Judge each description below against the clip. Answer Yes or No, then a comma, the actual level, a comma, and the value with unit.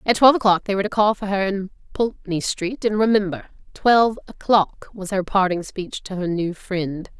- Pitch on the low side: No, high, 195 Hz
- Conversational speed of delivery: Yes, average, 190 wpm